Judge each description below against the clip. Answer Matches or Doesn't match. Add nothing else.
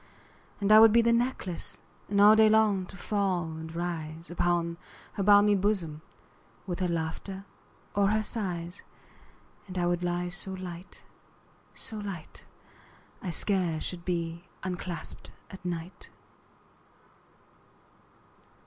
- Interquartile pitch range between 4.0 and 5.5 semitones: Doesn't match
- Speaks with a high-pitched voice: Doesn't match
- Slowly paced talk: Matches